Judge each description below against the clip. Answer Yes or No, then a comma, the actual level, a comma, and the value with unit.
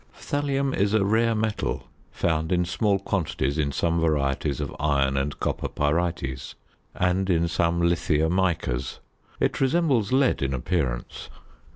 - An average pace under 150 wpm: Yes, average, 140 wpm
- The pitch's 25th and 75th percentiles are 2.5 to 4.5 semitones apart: No, wide, 5.6 semitones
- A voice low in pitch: Yes, very low, 85 Hz